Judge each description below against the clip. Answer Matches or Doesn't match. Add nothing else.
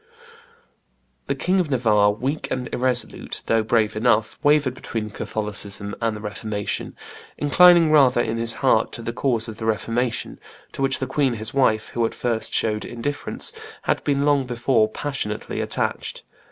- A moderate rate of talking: Matches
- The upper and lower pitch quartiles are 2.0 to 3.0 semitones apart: Doesn't match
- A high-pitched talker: Doesn't match